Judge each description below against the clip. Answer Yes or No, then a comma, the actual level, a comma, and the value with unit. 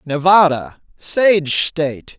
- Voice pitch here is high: No, medium, 165 Hz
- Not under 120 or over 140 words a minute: No, slow, 80 wpm